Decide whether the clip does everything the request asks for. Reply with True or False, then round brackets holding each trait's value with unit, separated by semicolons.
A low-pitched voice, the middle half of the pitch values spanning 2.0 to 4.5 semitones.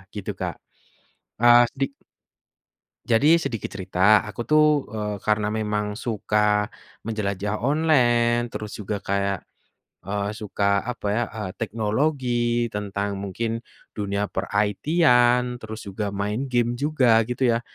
True (110 Hz; 2.8 semitones)